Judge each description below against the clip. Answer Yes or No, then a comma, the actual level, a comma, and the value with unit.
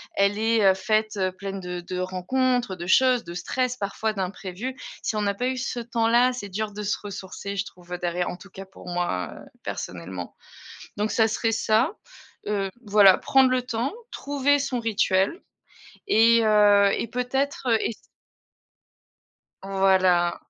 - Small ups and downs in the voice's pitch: No, average, 4.2 semitones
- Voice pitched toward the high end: Yes, high, 205 Hz